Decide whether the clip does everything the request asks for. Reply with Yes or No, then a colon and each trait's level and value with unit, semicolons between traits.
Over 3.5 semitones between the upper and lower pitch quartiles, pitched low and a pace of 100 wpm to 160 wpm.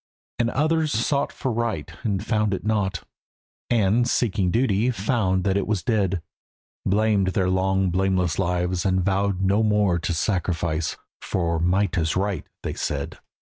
No: average, 3.0 semitones; very low, 95 Hz; average, 150 wpm